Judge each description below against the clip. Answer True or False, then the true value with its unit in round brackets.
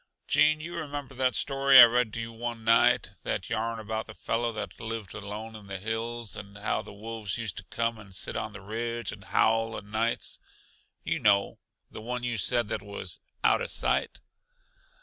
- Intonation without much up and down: True (2.1 semitones)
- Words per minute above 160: True (190 wpm)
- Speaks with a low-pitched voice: True (115 Hz)